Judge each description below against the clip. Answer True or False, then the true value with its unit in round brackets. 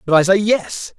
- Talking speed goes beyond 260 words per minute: False (245 wpm)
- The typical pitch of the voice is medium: True (165 Hz)